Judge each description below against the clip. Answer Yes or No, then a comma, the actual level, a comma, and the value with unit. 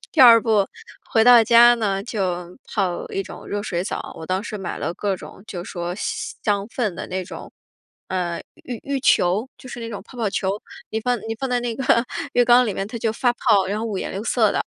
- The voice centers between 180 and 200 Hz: No, high, 215 Hz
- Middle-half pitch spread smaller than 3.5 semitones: No, average, 3.9 semitones